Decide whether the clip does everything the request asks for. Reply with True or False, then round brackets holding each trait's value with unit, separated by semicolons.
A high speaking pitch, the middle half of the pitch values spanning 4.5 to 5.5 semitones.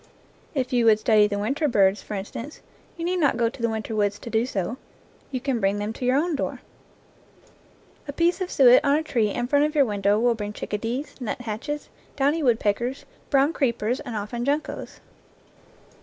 True (240 Hz; 4.9 semitones)